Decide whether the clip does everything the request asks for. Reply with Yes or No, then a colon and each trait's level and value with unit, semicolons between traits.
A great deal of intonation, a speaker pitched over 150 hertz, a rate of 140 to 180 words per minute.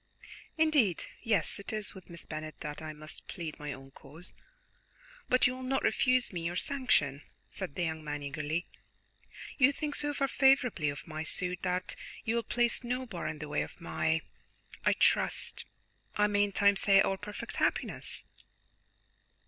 Yes: wide, 7.6 semitones; medium, 185 Hz; average, 175 wpm